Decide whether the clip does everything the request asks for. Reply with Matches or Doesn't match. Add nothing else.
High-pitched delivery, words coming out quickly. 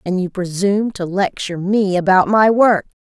Doesn't match